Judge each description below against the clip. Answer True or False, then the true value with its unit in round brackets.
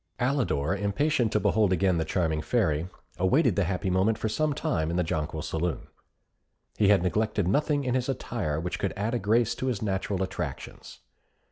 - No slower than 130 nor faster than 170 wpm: False (180 wpm)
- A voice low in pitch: True (100 Hz)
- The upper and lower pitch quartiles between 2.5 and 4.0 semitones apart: False (5.1 semitones)